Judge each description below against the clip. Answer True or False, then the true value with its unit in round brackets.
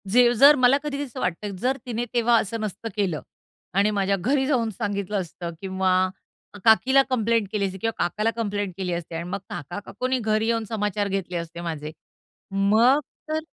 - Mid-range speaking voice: False (210 Hz)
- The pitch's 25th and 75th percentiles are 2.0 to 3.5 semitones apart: False (4.0 semitones)